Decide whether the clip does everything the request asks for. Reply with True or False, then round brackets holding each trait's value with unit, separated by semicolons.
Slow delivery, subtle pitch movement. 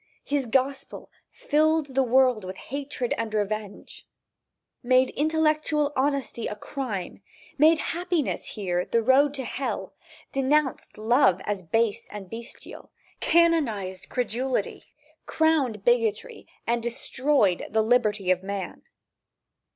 False (110 wpm; 5.2 semitones)